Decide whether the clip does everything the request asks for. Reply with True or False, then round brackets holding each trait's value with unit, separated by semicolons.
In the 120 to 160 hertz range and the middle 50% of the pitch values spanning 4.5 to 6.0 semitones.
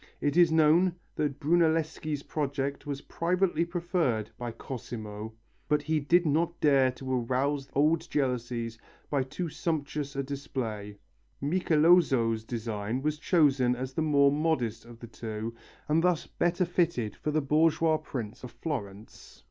True (140 Hz; 4.8 semitones)